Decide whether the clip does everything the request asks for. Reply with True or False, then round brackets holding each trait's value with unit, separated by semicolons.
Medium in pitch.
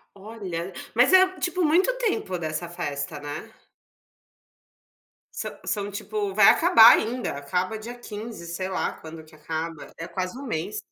False (195 Hz)